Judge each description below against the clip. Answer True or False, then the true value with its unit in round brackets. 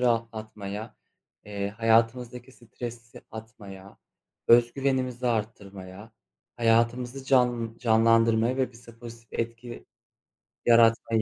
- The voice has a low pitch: True (115 Hz)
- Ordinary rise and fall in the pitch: False (1.4 semitones)